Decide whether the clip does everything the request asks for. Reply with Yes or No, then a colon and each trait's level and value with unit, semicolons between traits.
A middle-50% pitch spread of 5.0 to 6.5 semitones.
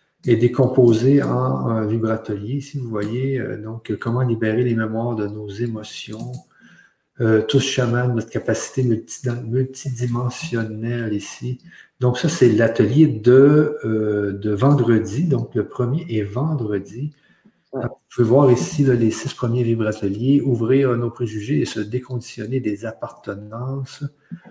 No: average, 3.1 semitones